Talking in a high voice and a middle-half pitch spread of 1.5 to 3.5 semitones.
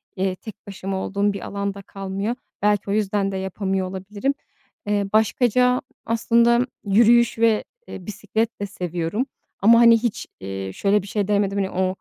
Yes: high, 200 Hz; average, 2.7 semitones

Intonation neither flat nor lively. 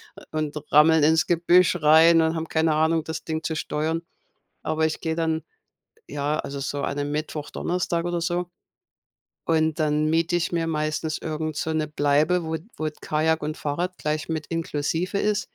No: narrow, 1.4 semitones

